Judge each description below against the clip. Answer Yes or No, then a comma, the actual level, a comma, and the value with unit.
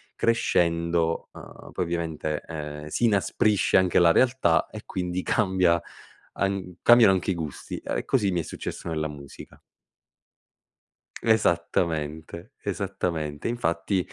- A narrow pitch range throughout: No, average, 3.2 semitones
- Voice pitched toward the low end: Yes, very low, 85 Hz